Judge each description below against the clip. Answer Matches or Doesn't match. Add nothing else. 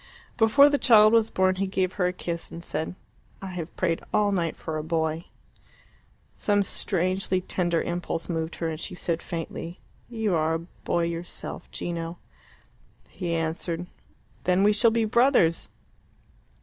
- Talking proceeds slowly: Doesn't match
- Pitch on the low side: Doesn't match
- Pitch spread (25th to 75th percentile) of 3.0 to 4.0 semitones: Matches